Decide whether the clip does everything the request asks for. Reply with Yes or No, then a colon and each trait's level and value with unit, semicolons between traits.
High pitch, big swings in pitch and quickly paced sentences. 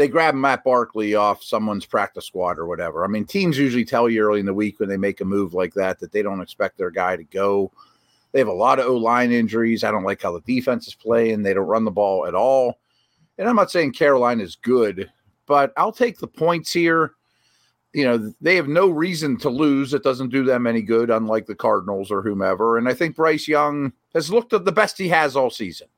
No: low, 120 Hz; wide, 6.0 semitones; fast, 240 wpm